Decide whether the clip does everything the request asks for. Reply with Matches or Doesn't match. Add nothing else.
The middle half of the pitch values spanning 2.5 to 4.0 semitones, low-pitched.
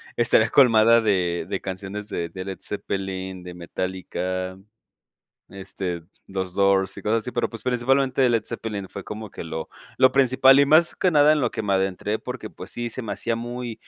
Doesn't match